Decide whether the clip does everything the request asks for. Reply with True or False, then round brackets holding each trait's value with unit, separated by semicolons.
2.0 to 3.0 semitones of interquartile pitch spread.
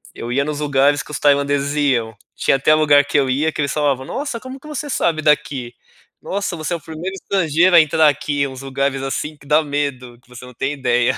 True (2.5 semitones)